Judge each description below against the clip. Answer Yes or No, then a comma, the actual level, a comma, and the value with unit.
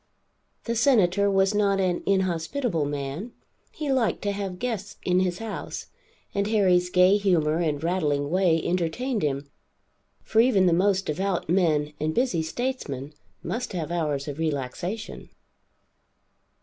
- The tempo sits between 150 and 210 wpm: No, slow, 135 wpm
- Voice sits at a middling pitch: Yes, medium, 180 Hz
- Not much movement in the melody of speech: No, average, 4.4 semitones